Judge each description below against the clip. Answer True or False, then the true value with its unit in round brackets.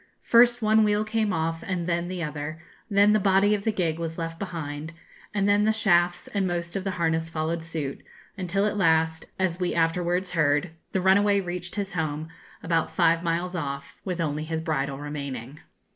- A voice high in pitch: False (170 Hz)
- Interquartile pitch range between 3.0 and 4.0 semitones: True (3.4 semitones)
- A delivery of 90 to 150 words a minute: False (190 wpm)